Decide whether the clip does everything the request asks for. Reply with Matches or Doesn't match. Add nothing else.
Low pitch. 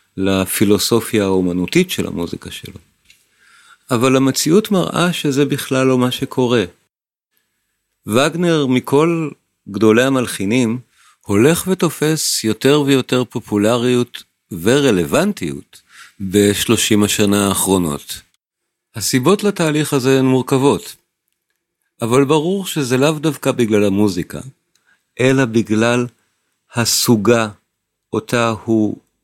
Matches